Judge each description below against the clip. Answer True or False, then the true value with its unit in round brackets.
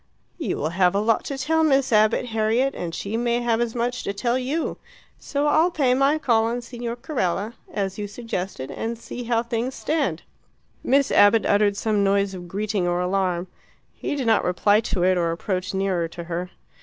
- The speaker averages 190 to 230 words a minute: True (195 wpm)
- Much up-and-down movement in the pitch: False (4.3 semitones)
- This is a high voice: True (220 Hz)